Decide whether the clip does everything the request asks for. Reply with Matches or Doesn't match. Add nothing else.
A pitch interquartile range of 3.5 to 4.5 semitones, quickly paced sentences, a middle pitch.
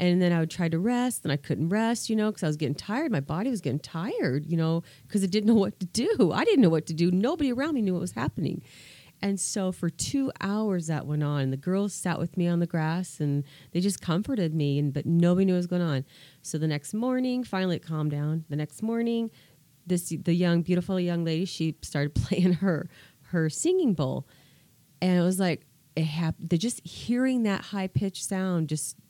Matches